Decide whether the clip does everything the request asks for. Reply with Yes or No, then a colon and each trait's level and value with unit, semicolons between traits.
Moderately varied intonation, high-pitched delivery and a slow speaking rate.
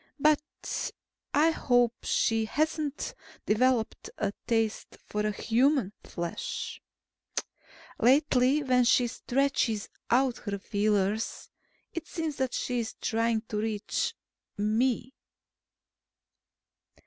Yes: average, 4.0 semitones; high, 240 Hz; slow, 90 wpm